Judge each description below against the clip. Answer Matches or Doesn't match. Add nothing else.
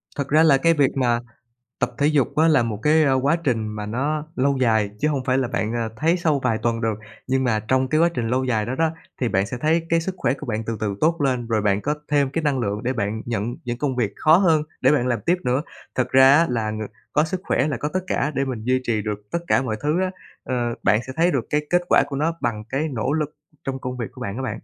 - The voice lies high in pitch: Doesn't match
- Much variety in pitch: Doesn't match